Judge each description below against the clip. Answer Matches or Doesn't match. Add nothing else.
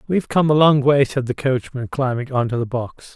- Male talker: Matches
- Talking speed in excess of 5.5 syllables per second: Doesn't match